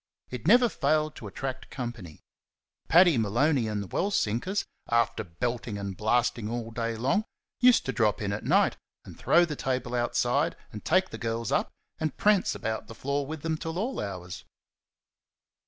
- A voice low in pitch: Yes, low, 120 Hz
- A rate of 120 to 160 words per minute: No, average, 170 wpm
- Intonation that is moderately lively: No, wide, 6.1 semitones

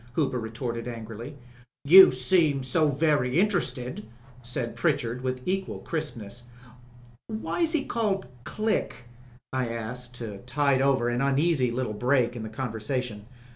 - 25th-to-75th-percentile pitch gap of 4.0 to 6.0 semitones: Yes, average, 4.3 semitones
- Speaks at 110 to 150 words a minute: Yes, slow, 135 wpm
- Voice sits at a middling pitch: No, low, 130 Hz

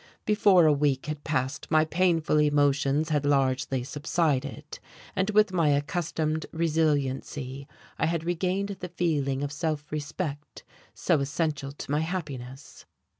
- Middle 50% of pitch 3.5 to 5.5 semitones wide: No, average, 2.8 semitones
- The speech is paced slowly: Yes, slow, 130 wpm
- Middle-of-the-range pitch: Yes, medium, 150 Hz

